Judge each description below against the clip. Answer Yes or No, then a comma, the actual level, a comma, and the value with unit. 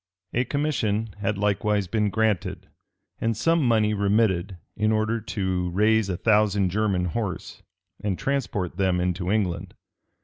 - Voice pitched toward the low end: Yes, low, 105 Hz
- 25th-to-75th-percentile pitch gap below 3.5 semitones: Yes, average, 2.7 semitones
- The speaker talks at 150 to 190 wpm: No, slow, 135 wpm